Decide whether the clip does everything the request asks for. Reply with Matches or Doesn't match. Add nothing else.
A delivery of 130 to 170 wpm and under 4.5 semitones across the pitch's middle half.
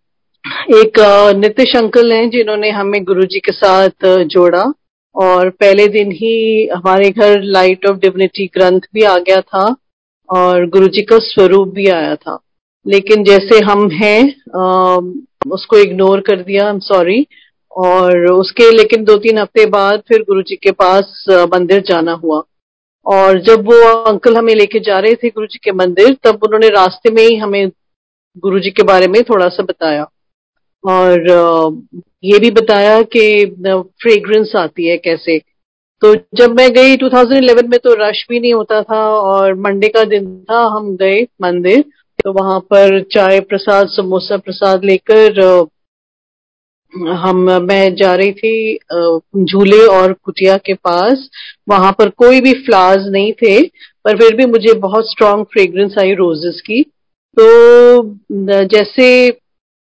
Matches